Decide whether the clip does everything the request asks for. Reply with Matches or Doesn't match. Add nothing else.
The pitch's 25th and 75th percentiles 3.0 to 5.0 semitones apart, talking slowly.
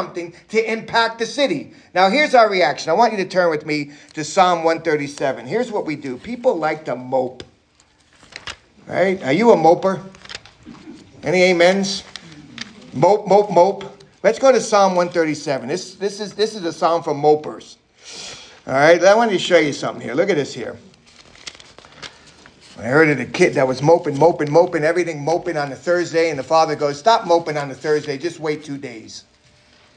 Doesn't match